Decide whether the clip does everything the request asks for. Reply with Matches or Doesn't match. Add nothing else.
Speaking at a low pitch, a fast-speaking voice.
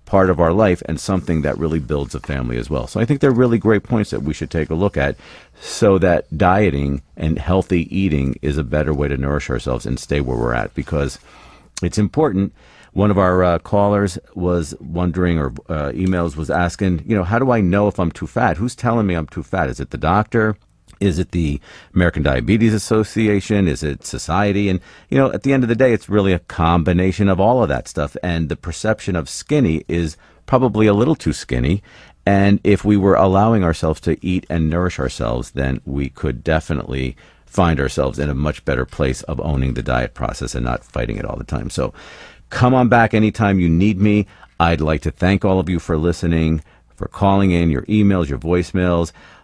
Matches